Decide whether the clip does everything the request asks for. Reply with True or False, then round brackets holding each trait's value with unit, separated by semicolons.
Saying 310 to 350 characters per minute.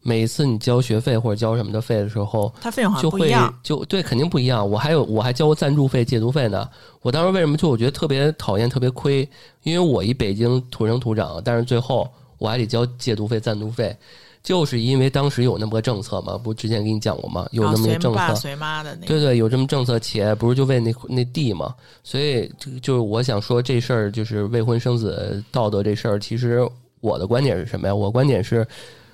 True (340 characters per minute)